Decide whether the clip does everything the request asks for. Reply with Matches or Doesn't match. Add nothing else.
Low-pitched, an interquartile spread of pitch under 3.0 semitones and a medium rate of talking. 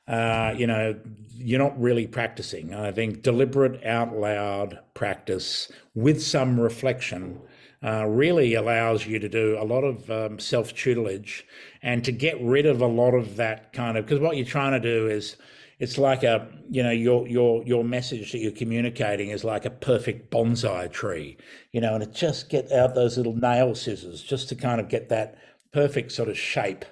Matches